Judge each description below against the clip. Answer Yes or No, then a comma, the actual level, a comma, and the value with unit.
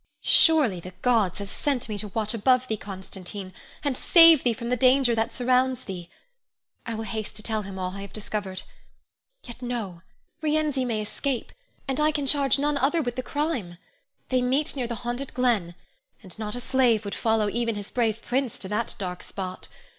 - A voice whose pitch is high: Yes, high, 235 Hz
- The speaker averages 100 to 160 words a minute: No, average, 190 wpm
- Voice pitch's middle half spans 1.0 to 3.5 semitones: No, average, 4.2 semitones